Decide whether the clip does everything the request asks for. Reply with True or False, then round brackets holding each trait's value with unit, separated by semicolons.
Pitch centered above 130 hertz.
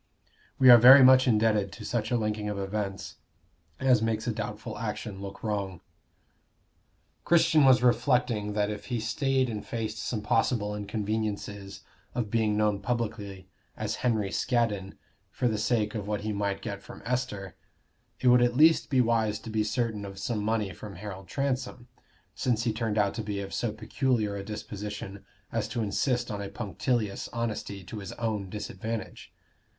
False (110 Hz)